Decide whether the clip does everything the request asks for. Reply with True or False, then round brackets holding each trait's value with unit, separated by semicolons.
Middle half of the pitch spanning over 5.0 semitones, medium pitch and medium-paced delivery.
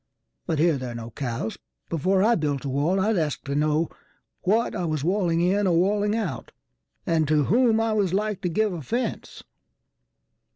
True (5.6 semitones; 170 Hz; 165 wpm)